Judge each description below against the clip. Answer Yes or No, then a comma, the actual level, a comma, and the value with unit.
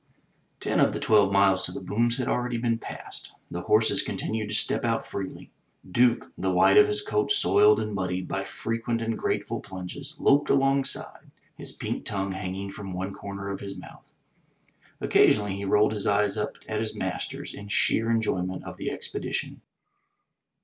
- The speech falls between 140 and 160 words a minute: No, average, 175 wpm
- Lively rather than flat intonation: No, average, 3.3 semitones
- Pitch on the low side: Yes, low, 105 Hz